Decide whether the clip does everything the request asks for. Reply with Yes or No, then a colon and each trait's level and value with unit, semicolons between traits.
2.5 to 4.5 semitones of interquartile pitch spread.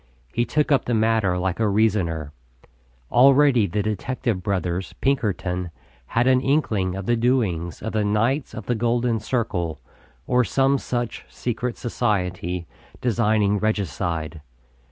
No: average, 4.9 semitones